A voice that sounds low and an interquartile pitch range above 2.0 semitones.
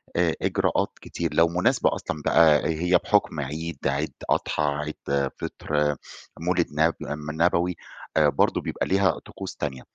Yes: very low, 80 Hz; average, 2.7 semitones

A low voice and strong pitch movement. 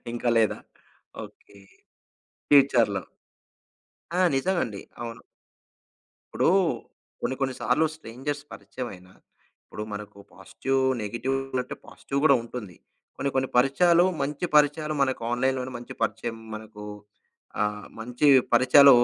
No: low, 125 Hz; average, 4.1 semitones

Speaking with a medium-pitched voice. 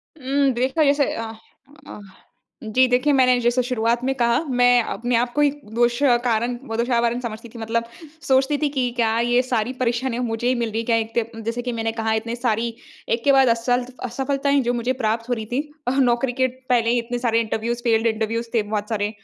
No: high, 240 Hz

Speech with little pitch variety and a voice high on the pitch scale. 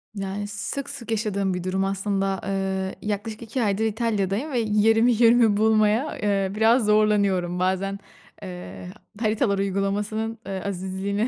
Yes: narrow, 2.3 semitones; high, 205 Hz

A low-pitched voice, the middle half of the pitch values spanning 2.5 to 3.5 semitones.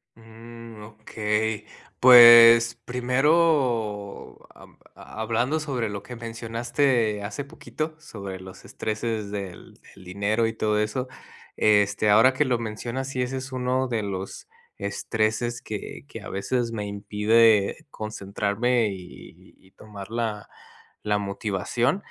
Yes: low, 110 Hz; average, 2.8 semitones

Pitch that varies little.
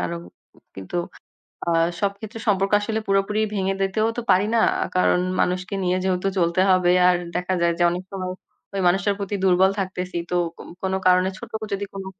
Yes: narrow, 1.5 semitones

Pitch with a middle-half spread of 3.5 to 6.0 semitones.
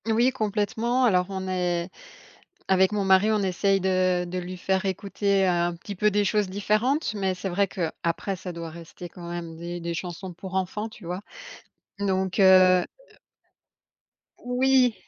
No: average, 2.7 semitones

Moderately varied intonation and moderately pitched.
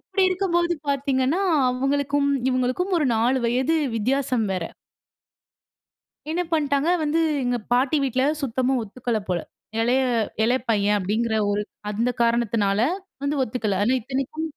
No: average, 3.9 semitones; very high, 255 Hz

